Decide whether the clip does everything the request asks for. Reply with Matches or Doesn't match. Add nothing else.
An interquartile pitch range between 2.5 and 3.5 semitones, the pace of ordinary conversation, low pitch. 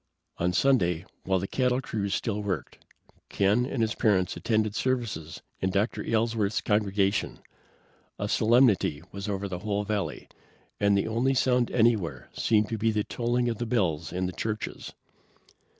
Matches